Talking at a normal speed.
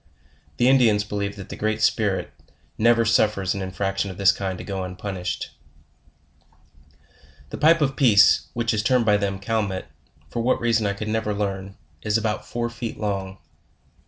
Yes: average, 175 wpm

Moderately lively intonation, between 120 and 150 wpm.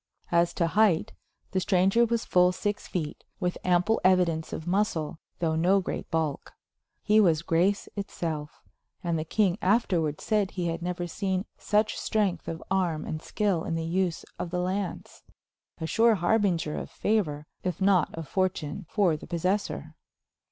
No: average, 3.3 semitones; average, 160 wpm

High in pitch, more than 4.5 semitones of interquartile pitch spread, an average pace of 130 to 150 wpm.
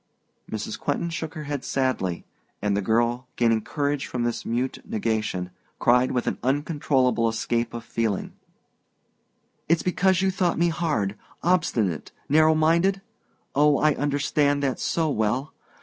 No: low, 135 Hz; average, 5.2 semitones; average, 140 wpm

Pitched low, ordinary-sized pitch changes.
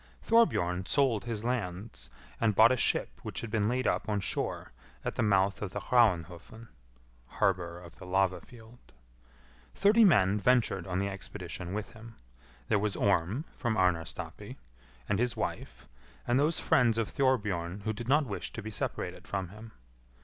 Yes: low, 105 Hz; average, 4.1 semitones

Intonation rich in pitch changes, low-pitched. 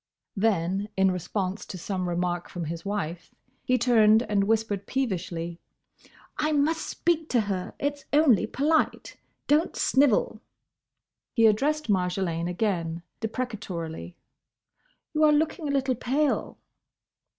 No: wide, 7.3 semitones; high, 210 Hz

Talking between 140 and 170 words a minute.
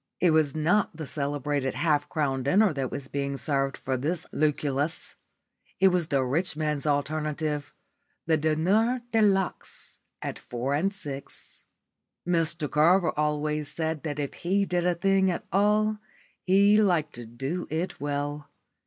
Yes: average, 150 wpm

